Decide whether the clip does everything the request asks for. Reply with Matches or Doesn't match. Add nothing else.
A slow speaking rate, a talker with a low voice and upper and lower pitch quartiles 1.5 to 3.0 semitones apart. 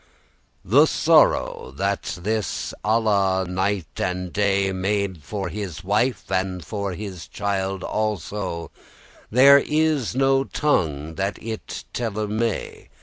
Matches